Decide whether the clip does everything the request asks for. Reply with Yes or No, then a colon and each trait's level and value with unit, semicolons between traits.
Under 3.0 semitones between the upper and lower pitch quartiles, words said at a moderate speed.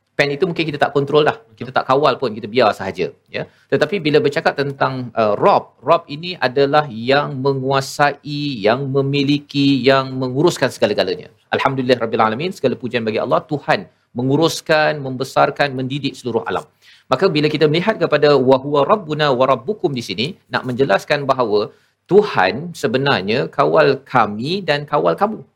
No: narrow, 2.4 semitones; fast, 155 wpm